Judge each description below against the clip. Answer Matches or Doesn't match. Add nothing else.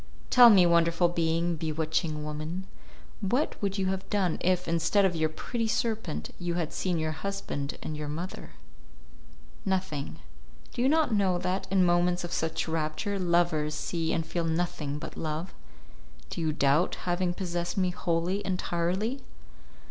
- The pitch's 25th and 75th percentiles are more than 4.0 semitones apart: Doesn't match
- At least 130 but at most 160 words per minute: Matches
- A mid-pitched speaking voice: Matches